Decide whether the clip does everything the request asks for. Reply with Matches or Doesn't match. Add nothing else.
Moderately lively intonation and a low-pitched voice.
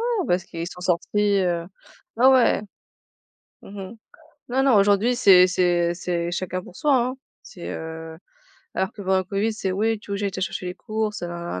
Doesn't match